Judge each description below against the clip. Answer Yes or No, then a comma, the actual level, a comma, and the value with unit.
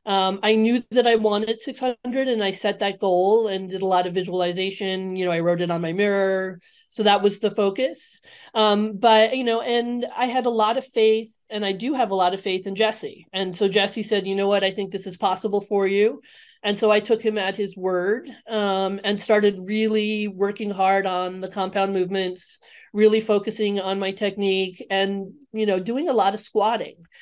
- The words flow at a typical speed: No, fast, 215 wpm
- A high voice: Yes, high, 205 Hz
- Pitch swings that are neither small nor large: No, narrow, 2.3 semitones